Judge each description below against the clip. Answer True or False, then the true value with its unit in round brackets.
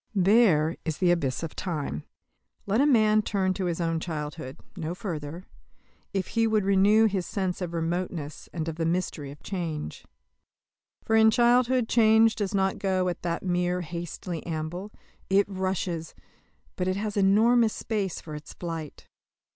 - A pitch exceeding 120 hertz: True (185 Hz)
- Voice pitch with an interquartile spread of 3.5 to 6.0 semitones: True (4.0 semitones)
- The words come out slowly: False (160 wpm)